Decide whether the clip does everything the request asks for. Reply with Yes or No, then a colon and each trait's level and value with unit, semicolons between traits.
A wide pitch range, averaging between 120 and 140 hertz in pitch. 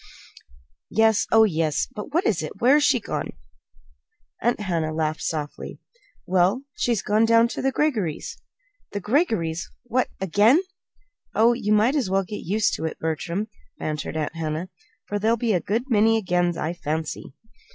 No: wide, 5.8 semitones; high, 205 Hz